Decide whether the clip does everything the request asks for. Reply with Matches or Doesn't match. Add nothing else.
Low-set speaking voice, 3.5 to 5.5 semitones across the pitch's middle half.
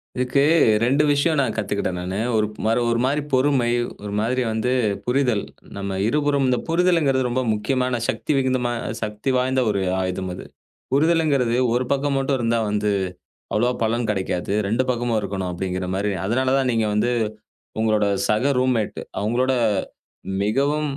Matches